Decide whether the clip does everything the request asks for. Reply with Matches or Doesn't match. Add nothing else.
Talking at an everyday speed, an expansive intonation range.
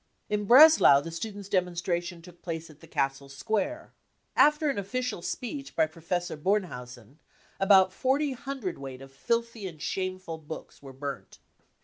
Matches